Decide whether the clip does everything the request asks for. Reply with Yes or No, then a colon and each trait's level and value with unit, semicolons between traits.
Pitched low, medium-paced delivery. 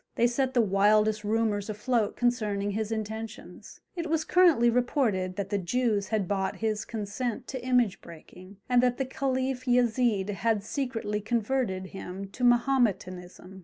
No: high, 220 Hz; average, 150 wpm